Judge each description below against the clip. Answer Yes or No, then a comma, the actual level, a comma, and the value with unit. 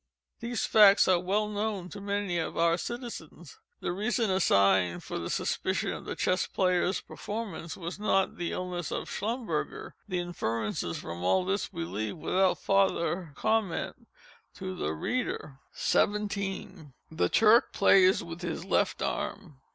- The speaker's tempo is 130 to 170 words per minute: Yes, average, 145 wpm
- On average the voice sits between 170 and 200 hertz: Yes, medium, 185 Hz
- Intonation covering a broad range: No, average, 3.9 semitones